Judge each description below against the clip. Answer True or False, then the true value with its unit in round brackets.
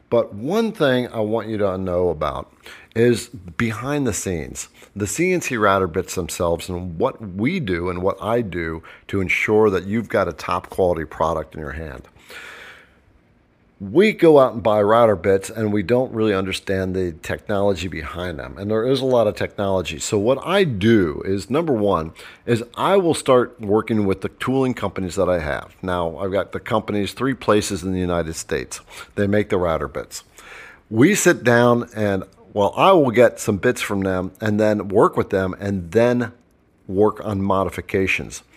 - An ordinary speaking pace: True (185 wpm)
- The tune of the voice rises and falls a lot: False (4.2 semitones)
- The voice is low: True (100 Hz)